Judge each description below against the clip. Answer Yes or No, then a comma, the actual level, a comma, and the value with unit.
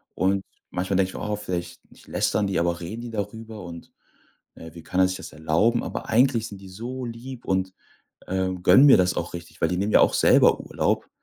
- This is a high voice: No, very low, 95 Hz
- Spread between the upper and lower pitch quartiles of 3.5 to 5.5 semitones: Yes, average, 4.0 semitones